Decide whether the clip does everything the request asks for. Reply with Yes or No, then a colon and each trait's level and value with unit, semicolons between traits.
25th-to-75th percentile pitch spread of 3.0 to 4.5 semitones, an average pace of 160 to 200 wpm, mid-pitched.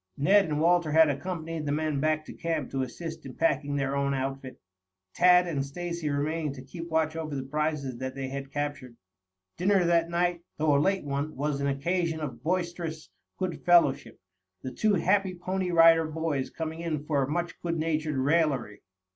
Yes: average, 3.3 semitones; average, 180 wpm; medium, 155 Hz